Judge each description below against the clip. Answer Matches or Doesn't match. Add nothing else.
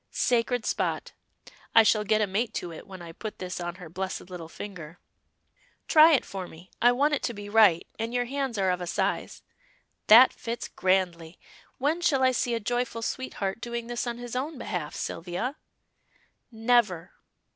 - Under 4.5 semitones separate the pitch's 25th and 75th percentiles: Doesn't match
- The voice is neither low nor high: Doesn't match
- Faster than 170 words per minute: Matches